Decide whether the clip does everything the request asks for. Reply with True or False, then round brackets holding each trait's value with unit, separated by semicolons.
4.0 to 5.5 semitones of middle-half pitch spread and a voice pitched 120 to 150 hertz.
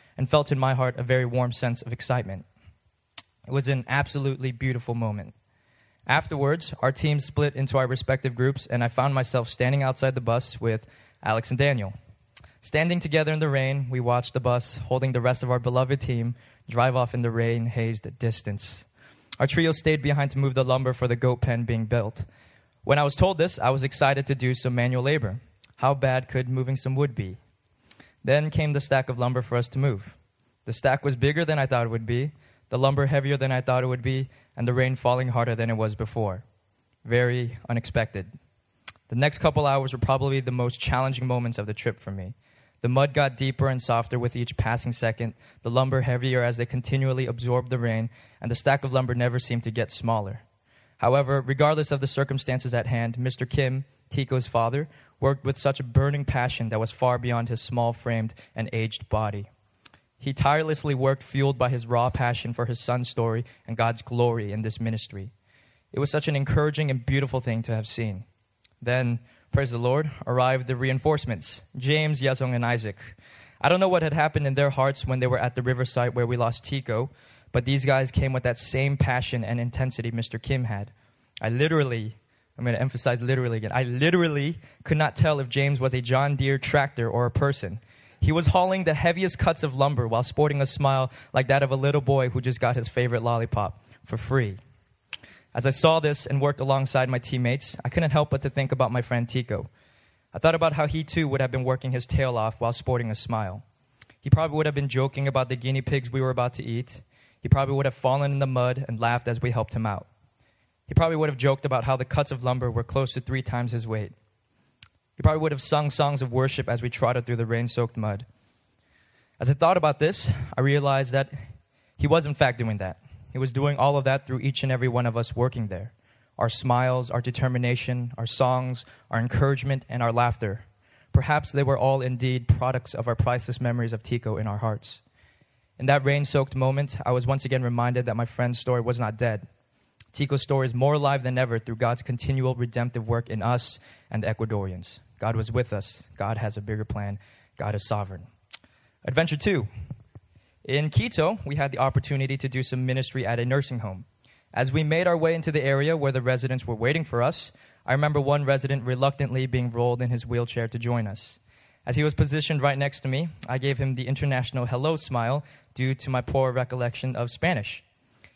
False (2.7 semitones; 125 Hz)